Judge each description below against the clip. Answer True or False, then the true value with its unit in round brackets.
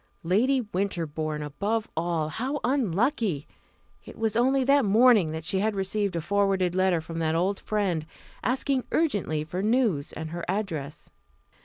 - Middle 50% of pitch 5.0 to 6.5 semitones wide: True (5.6 semitones)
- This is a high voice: True (195 Hz)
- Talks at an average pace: True (150 wpm)